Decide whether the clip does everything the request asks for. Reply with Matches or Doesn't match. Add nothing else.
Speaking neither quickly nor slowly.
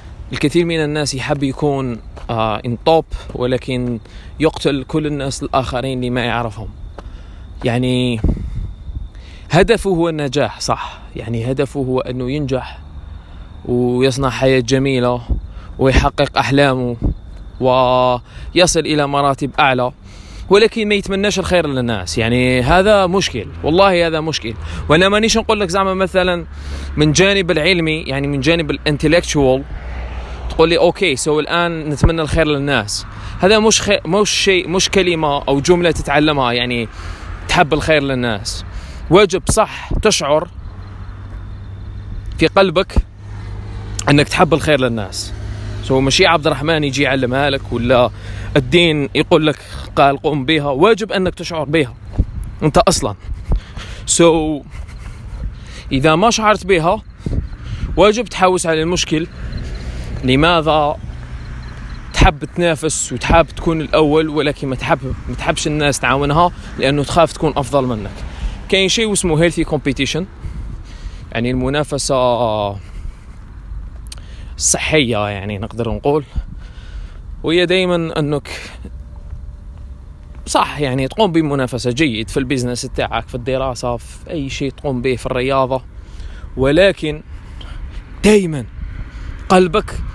Matches